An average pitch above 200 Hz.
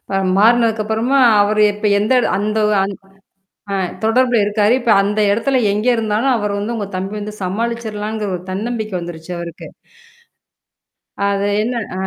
Yes: high, 215 Hz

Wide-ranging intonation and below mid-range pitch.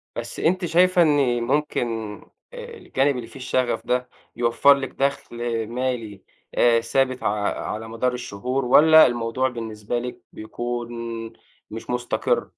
No: average, 2.8 semitones; low, 125 Hz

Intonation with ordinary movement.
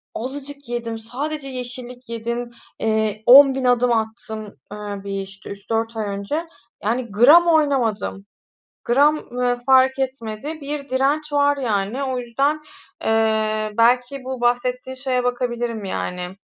Yes: average, 3.5 semitones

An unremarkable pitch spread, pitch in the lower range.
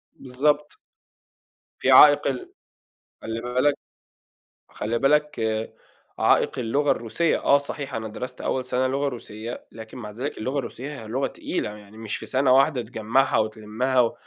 Yes: average, 3.6 semitones; low, 125 Hz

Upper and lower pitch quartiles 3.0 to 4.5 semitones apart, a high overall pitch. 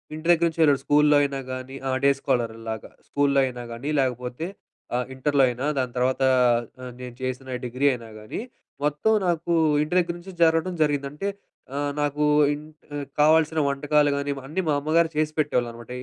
No: average, 3.3 semitones; medium, 145 Hz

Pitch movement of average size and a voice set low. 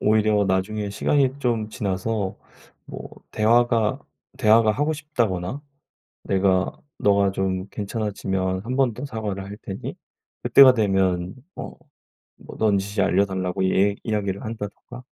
Yes: average, 3.1 semitones; low, 105 Hz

